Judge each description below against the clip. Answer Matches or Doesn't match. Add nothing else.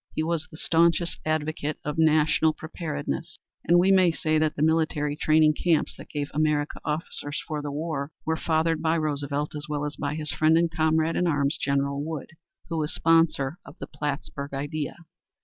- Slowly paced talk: Doesn't match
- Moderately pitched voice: Matches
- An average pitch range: Doesn't match